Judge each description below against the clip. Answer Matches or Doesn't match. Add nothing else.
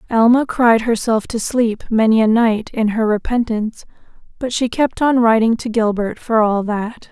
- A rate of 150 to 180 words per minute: Matches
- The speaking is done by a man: Doesn't match